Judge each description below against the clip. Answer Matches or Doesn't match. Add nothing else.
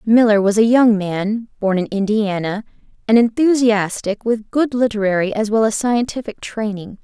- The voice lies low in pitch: Doesn't match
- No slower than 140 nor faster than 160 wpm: Matches